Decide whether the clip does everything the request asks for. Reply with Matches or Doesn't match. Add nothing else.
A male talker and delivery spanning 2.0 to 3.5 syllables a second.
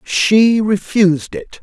Matches